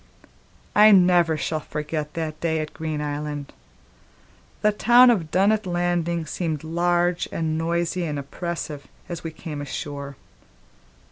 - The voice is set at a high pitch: No, medium, 165 Hz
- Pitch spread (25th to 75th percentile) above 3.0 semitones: No, narrow, 2.6 semitones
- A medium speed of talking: No, slow, 130 wpm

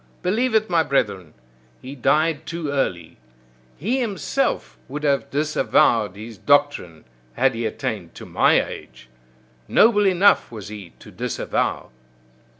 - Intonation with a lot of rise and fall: Yes, wide, 8.5 semitones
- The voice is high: No, medium, 145 Hz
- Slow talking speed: Yes, slow, 130 wpm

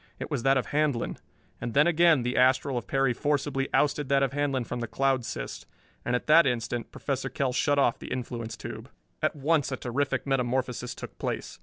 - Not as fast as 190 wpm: No, average, 200 wpm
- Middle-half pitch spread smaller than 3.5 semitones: Yes, narrow, 2.6 semitones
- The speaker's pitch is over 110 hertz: Yes, low, 135 Hz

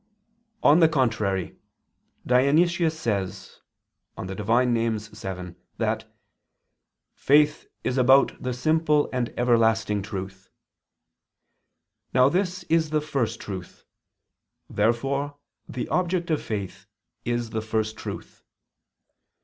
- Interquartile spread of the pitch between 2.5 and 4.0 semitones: No, wide, 5.6 semitones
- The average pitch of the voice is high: No, low, 120 Hz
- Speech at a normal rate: No, slow, 100 wpm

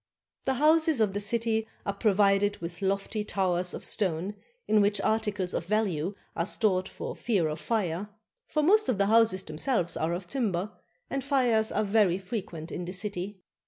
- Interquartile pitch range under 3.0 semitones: No, average, 3.5 semitones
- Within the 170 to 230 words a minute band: Yes, average, 175 wpm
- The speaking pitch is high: Yes, high, 205 Hz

